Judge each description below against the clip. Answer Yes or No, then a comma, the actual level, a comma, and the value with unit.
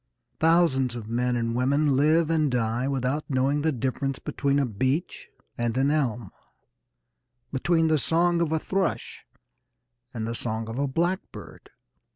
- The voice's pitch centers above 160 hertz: No, low, 135 Hz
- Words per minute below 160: Yes, average, 150 wpm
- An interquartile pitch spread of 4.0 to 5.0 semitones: Yes, average, 4.4 semitones